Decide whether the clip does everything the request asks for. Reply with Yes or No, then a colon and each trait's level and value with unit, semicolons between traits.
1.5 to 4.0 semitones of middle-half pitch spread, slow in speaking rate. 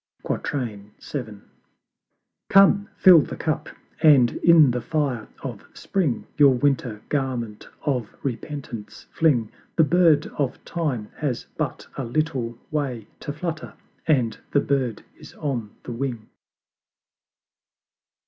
No: average, 4.4 semitones; slow, 115 wpm